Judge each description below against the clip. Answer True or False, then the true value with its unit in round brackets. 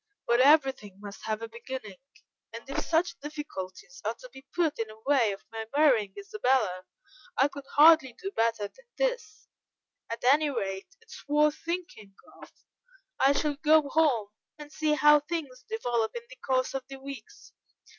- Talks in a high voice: True (270 Hz)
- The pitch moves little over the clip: False (5.2 semitones)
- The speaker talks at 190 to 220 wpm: False (165 wpm)